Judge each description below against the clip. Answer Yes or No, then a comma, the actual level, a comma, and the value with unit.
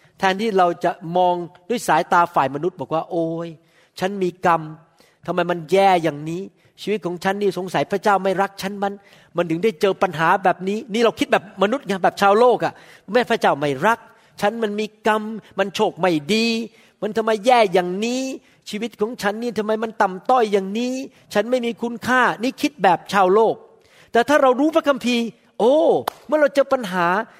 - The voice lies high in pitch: Yes, high, 200 Hz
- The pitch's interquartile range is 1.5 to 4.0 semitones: No, average, 4.6 semitones